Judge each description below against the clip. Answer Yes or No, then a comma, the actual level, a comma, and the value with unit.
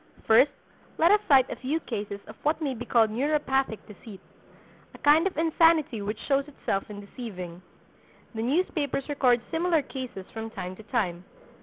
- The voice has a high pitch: Yes, very high, 255 Hz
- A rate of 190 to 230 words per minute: No, average, 160 wpm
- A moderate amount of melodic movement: No, wide, 5.7 semitones